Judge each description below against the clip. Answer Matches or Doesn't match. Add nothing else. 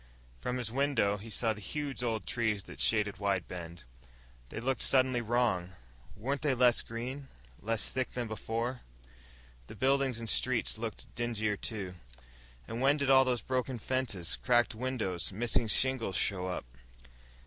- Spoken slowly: Doesn't match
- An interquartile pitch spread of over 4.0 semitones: Doesn't match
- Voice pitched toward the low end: Matches